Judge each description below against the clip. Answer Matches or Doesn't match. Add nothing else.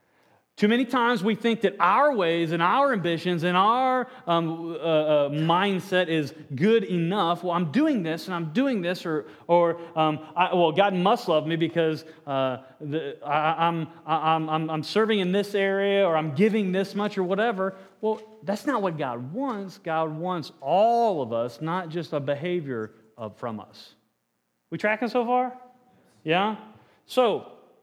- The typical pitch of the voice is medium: Matches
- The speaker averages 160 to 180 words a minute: Matches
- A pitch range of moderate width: Matches